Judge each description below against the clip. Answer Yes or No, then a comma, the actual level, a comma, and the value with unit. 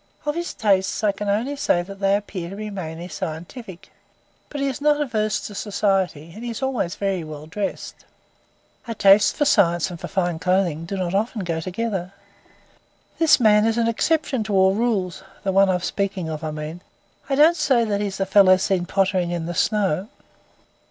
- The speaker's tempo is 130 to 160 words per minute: No, average, 190 wpm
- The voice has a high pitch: Yes, high, 195 Hz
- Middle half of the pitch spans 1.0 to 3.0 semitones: No, average, 3.8 semitones